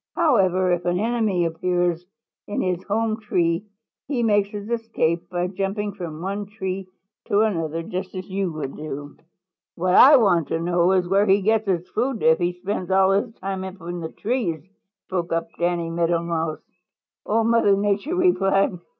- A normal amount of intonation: Yes, average, 3.2 semitones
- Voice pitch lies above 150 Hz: Yes, medium, 185 Hz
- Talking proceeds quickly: No, average, 175 wpm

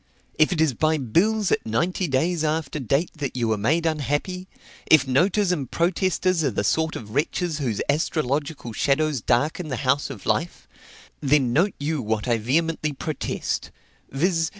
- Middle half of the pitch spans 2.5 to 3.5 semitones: No, average, 4.2 semitones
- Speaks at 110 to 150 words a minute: No, average, 165 wpm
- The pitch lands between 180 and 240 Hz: No, medium, 150 Hz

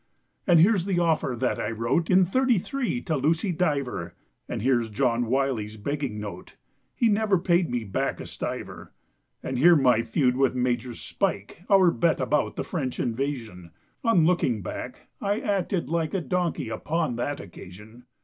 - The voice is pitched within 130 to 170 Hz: Yes, medium, 140 Hz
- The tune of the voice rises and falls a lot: Yes, wide, 6.7 semitones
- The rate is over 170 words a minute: No, average, 160 wpm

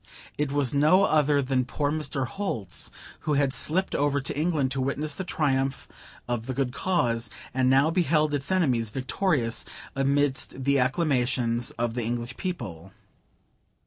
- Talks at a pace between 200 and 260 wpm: No, average, 150 wpm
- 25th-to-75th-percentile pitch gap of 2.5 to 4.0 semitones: Yes, average, 3.4 semitones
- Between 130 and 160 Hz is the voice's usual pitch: Yes, low, 135 Hz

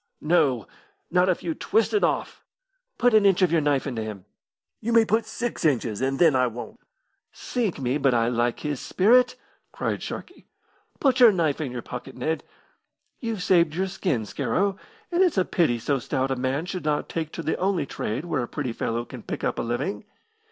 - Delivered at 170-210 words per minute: Yes, average, 200 wpm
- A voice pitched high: No, medium, 155 Hz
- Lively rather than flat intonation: Yes, wide, 7.2 semitones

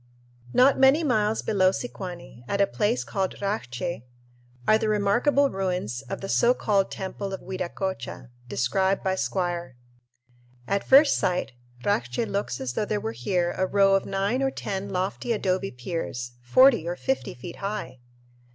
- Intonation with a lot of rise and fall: No, average, 3.5 semitones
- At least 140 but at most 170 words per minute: Yes, average, 155 wpm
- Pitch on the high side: Yes, high, 195 Hz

